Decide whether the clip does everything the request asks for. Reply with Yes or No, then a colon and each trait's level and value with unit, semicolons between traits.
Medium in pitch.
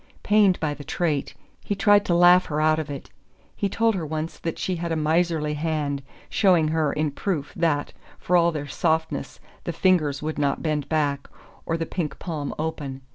Yes: medium, 160 Hz